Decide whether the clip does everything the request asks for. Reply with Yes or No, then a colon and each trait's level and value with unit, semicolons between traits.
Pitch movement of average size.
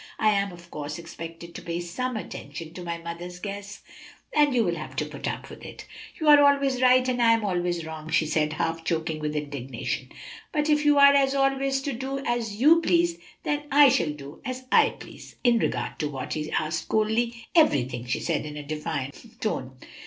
No: wide, 8.6 semitones